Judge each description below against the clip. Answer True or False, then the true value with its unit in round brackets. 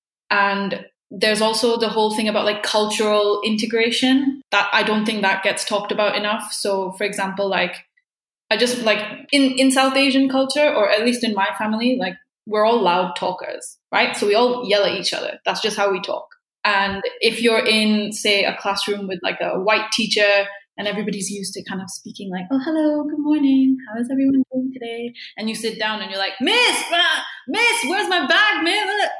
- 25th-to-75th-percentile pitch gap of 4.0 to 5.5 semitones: True (4.6 semitones)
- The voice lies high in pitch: True (220 Hz)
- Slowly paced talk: False (200 wpm)